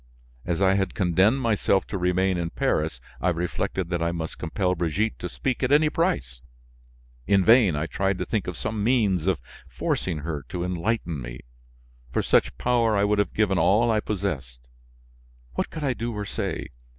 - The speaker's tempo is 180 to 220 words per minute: Yes, average, 185 wpm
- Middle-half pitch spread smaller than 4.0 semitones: No, average, 4.3 semitones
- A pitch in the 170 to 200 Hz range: No, very low, 95 Hz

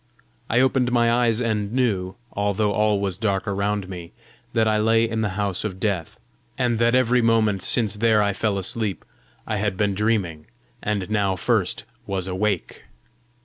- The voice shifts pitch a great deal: No, average, 2.7 semitones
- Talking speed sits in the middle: Yes, average, 170 wpm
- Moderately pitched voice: No, low, 105 Hz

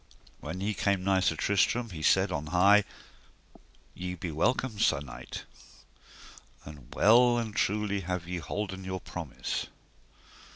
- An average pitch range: Yes, average, 3.8 semitones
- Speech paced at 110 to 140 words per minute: Yes, slow, 135 wpm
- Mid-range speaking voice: No, very low, 95 Hz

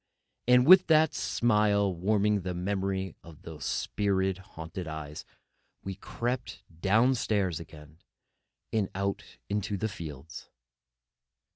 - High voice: No, very low, 95 Hz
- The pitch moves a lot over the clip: No, average, 4.0 semitones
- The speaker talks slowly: Yes, slow, 115 wpm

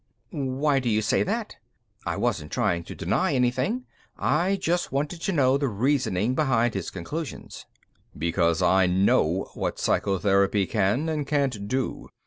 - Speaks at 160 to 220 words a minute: No, average, 145 wpm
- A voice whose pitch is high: No, low, 125 Hz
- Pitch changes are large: Yes, wide, 7.3 semitones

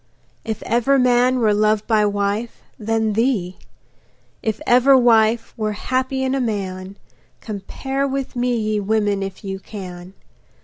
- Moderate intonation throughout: Yes, average, 3.4 semitones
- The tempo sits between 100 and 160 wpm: Yes, average, 140 wpm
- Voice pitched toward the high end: Yes, high, 220 Hz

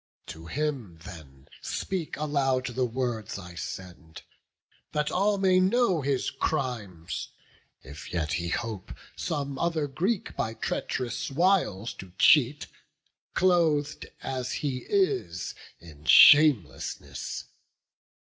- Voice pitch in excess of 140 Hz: No, low, 130 Hz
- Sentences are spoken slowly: Yes, slow, 110 wpm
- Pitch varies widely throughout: Yes, wide, 8.9 semitones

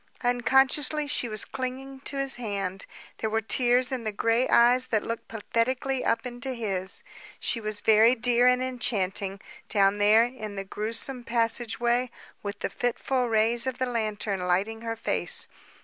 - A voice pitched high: Yes, high, 230 Hz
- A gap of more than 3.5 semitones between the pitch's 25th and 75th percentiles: No, average, 2.9 semitones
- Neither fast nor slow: Yes, average, 160 wpm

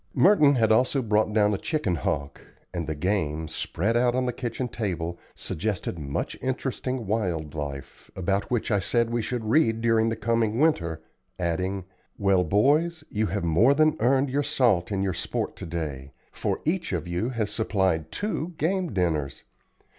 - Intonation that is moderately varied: No, wide, 6.5 semitones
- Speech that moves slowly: No, average, 170 wpm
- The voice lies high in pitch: No, low, 105 Hz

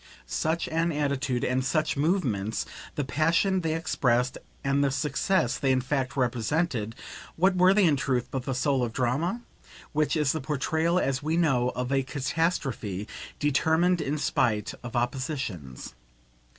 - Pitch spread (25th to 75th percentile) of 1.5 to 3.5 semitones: No, average, 4.2 semitones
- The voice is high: No, medium, 140 Hz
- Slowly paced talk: No, average, 150 wpm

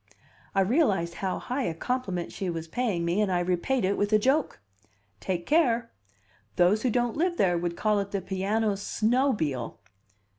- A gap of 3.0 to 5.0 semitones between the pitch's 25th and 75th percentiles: No, wide, 5.5 semitones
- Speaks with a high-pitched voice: Yes, high, 200 Hz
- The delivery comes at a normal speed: Yes, average, 175 wpm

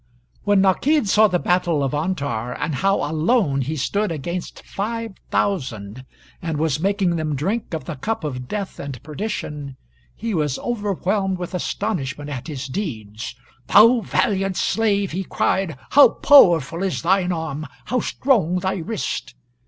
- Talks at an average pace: Yes, average, 155 wpm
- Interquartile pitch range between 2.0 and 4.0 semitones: No, wide, 5.6 semitones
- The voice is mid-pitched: Yes, medium, 175 Hz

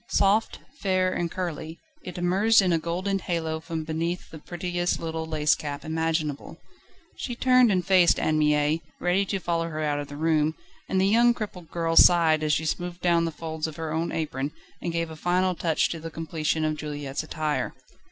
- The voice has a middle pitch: Yes, medium, 165 Hz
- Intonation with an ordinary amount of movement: No, narrow, 2.3 semitones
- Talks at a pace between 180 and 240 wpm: Yes, average, 195 wpm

